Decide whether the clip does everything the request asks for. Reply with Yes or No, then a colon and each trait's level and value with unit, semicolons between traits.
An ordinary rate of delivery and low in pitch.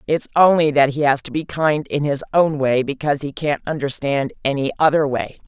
No: average, 195 wpm; medium, 145 Hz